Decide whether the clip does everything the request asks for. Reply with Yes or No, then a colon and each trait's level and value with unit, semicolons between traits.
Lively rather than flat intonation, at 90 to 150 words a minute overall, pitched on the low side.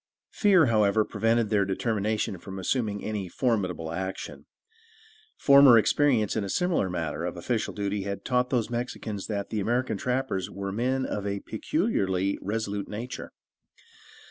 No: average, 3.8 semitones; average, 145 wpm; low, 105 Hz